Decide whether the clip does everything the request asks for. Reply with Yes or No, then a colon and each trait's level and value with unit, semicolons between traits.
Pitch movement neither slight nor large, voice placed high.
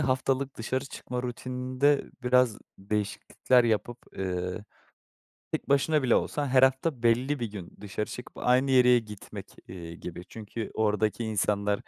No: average, 3.6 semitones; low, 120 Hz